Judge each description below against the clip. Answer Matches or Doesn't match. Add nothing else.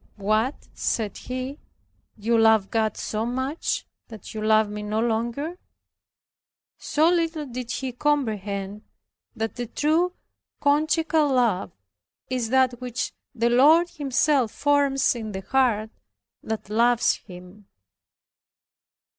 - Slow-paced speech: Matches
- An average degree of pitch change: Matches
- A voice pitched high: Matches